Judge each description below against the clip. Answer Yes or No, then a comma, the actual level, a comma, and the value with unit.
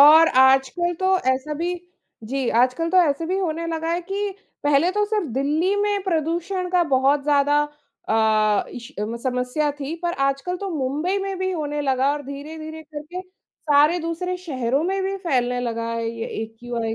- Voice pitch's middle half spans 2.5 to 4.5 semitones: No, average, 5.1 semitones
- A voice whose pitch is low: No, very high, 300 Hz